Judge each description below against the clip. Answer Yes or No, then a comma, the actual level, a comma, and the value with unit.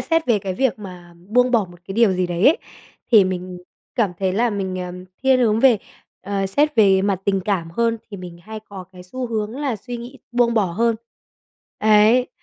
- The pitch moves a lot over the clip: No, average, 4.0 semitones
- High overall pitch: Yes, high, 210 Hz